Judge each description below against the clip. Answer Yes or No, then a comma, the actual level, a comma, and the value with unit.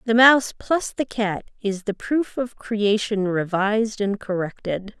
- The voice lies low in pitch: No, high, 215 Hz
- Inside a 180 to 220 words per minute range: No, average, 155 wpm